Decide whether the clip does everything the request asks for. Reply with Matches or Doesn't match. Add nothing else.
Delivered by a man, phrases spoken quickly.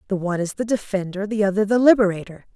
Doesn't match